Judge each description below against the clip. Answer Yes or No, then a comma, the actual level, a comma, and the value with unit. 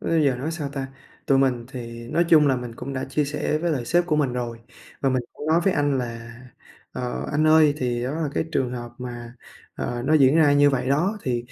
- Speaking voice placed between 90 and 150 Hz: Yes, low, 135 Hz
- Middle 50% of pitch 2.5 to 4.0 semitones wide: Yes, average, 3.7 semitones